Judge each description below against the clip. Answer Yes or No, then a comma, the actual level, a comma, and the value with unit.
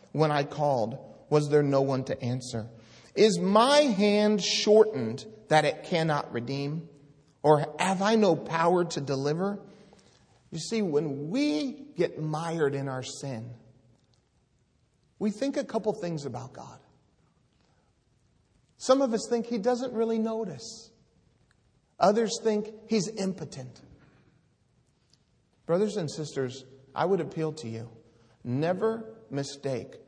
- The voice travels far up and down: Yes, wide, 7.8 semitones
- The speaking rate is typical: No, slow, 125 wpm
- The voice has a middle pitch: Yes, medium, 155 Hz